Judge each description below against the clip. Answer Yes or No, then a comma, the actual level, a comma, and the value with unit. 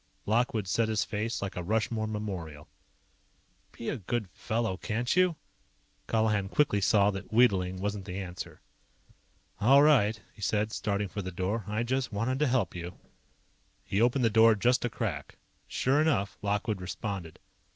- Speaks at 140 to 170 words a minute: Yes, average, 160 wpm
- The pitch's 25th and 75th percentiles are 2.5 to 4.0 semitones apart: Yes, average, 3.2 semitones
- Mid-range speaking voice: No, low, 105 Hz